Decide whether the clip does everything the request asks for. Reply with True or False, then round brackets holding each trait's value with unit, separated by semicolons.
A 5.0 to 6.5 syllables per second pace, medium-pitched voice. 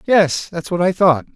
False (4.3 syllables/s; 175 Hz)